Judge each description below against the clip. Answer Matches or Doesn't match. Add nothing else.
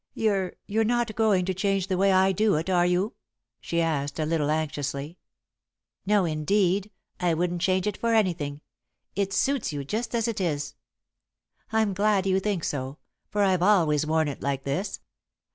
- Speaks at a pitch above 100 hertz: Matches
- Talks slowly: Doesn't match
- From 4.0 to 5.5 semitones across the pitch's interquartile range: Matches